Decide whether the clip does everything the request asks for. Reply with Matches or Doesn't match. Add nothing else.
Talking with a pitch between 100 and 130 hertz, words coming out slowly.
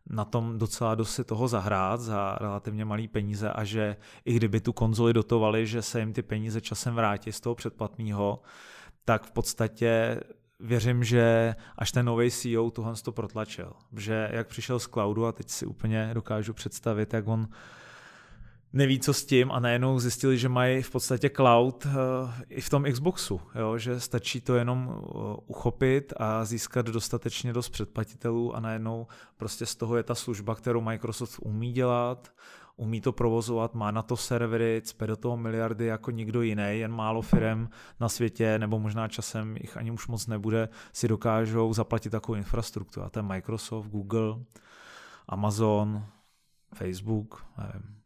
Doesn't match